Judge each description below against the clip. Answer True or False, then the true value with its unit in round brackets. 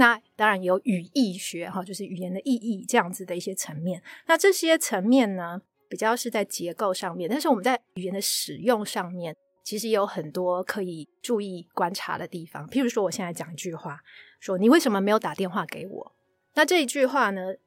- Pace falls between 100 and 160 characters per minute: False (315 characters per minute)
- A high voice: True (195 Hz)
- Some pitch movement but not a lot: True (4.7 semitones)